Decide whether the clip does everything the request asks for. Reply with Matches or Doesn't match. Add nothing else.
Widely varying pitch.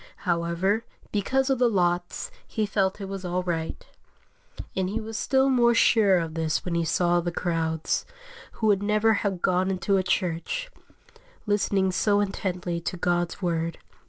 Doesn't match